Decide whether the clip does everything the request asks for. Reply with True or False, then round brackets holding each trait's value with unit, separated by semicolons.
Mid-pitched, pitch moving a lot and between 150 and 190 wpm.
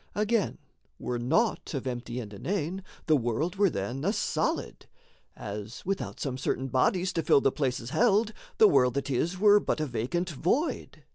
True (155 Hz; 7.8 semitones; 170 wpm)